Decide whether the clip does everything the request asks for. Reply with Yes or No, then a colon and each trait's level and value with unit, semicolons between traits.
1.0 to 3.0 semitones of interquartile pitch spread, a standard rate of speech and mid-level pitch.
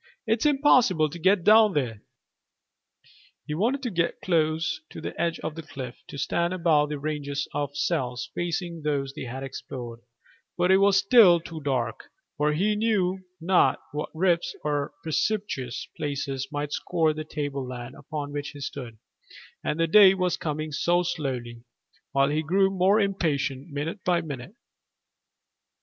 No: average, 4.4 semitones; average, 155 wpm; medium, 155 Hz